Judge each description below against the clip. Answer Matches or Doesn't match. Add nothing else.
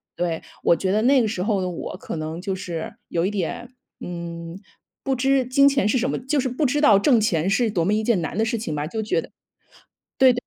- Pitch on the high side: Matches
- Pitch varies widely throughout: Matches